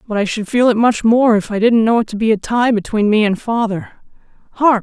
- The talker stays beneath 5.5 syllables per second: No, 5.7 syllables/s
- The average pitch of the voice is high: Yes, high, 225 Hz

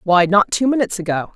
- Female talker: Yes, female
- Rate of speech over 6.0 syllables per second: Yes, 6.4 syllables/s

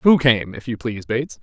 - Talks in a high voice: No, low, 125 Hz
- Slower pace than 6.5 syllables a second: Yes, 5.8 syllables/s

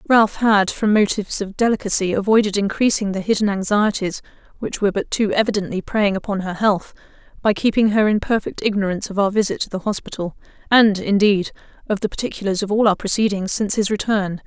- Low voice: No, high, 205 Hz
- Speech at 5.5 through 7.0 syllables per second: Yes, 6.0 syllables/s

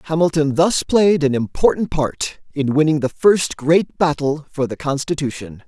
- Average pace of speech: Yes, average, 160 wpm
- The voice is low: No, medium, 150 Hz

